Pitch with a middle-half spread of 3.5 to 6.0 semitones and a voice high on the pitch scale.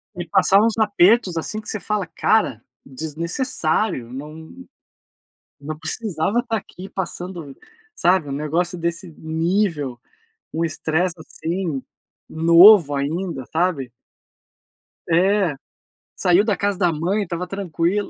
No: average, 3.8 semitones; medium, 175 Hz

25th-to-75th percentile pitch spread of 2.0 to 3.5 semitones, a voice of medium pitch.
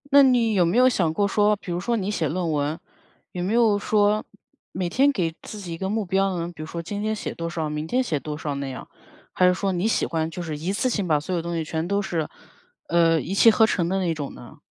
No: average, 4.1 semitones; medium, 180 Hz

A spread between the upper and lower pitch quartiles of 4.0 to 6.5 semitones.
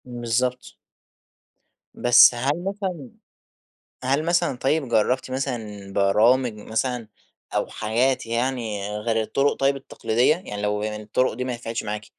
No: average, 3.5 semitones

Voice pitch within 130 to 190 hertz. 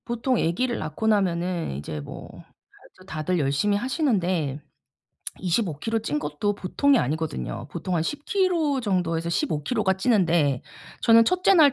Yes: medium, 185 Hz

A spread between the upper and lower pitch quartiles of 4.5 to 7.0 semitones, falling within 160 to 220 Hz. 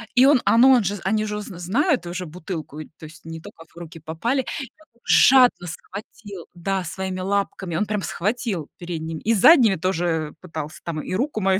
Yes: average, 5.0 semitones; high, 190 Hz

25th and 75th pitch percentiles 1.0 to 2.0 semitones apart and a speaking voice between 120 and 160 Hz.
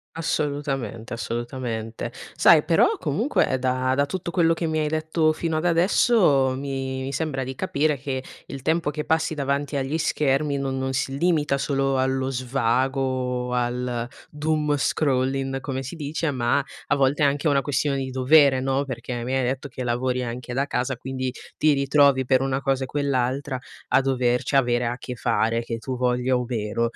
No: narrow, 2.4 semitones; low, 135 Hz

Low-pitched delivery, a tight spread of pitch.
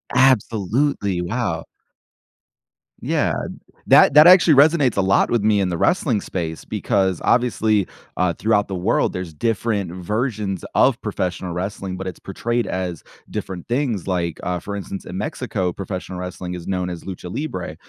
No: very low, 95 Hz; average, 4.3 semitones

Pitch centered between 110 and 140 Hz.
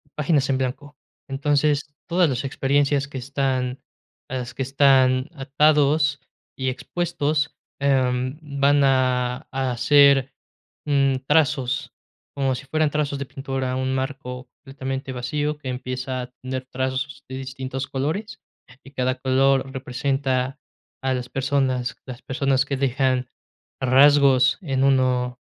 Yes: low, 135 Hz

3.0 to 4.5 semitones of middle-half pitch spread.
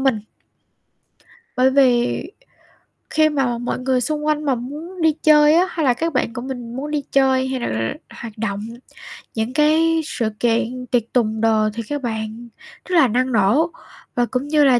Yes: average, 4.2 semitones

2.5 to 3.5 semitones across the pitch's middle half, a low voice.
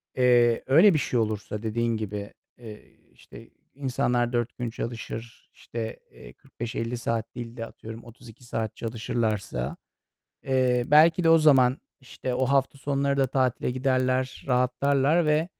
Yes: average, 2.8 semitones; low, 125 Hz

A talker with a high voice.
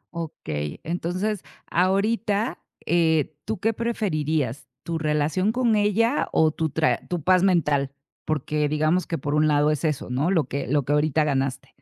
No: medium, 160 Hz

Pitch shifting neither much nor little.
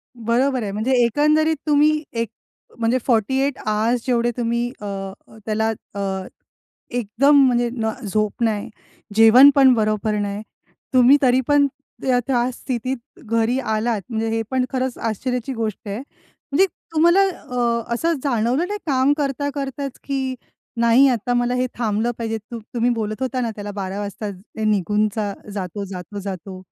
Yes: average, 3.5 semitones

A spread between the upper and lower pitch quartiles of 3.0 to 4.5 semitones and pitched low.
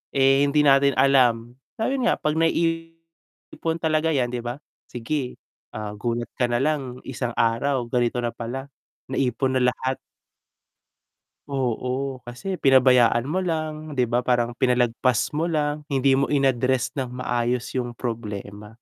Yes: average, 3.4 semitones; low, 130 Hz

